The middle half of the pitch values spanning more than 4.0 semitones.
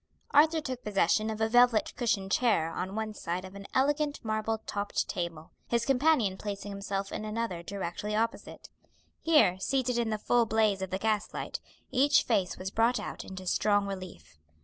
No: average, 3.7 semitones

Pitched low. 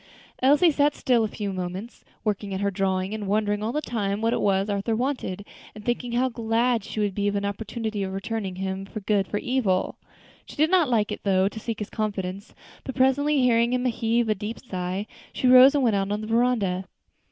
No: high, 215 Hz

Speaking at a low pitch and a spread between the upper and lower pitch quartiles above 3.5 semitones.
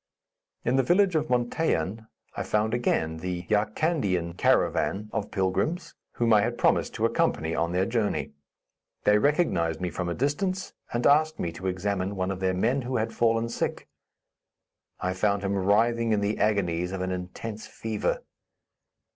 Yes: low, 105 Hz; average, 4.6 semitones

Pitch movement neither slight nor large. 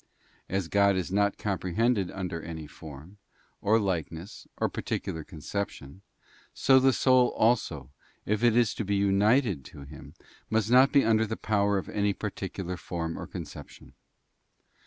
Yes: average, 4.3 semitones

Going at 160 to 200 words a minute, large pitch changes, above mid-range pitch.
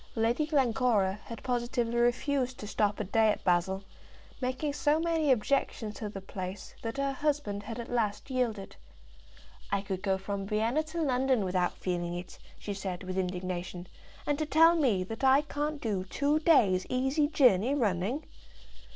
Yes: average, 165 wpm; wide, 5.9 semitones; high, 230 Hz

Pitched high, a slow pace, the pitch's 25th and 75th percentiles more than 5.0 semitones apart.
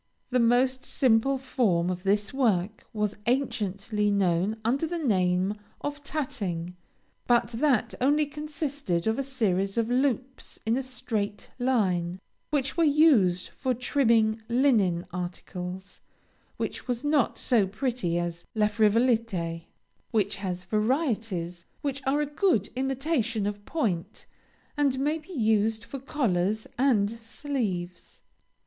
Yes: high, 225 Hz; slow, 130 wpm; wide, 5.5 semitones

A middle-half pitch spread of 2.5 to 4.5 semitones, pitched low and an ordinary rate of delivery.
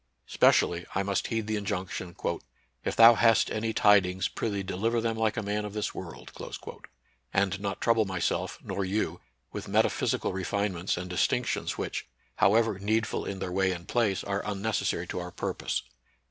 Yes: average, 2.8 semitones; low, 100 Hz; average, 170 wpm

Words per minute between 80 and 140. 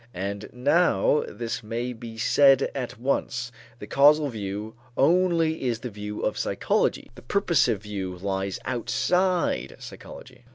Yes: slow, 135 wpm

